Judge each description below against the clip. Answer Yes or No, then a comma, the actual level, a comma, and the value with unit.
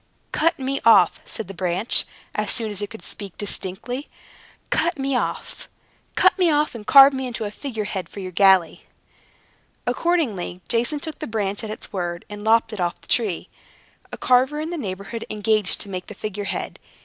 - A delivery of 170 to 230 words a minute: Yes, average, 185 wpm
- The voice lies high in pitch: Yes, high, 215 Hz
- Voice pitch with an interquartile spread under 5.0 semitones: No, average, 5.3 semitones